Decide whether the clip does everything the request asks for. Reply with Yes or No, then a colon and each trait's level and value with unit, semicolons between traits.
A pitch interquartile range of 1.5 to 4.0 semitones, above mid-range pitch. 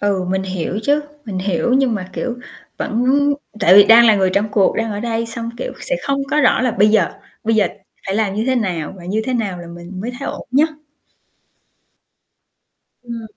Yes: average, 3.7 semitones; high, 215 Hz